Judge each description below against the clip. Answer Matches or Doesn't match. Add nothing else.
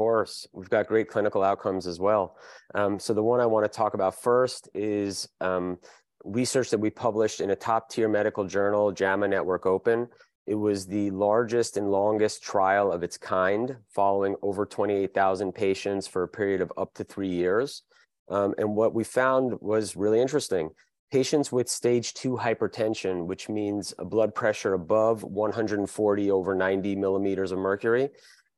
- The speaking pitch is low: Matches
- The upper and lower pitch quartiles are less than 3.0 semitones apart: Matches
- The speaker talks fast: Doesn't match